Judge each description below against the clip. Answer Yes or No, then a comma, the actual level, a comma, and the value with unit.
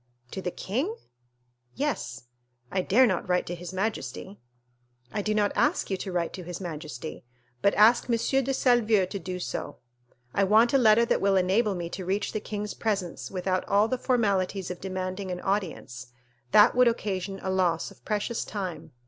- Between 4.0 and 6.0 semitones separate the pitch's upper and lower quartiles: No, average, 3.2 semitones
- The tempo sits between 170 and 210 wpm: Yes, average, 180 wpm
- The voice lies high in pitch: Yes, high, 195 Hz